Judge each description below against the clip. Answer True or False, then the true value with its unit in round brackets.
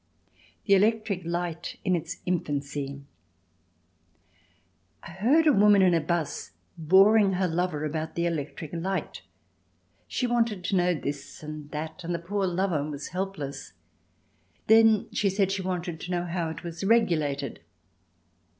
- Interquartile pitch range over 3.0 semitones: True (3.7 semitones)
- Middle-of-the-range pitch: True (175 Hz)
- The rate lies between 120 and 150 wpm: True (140 wpm)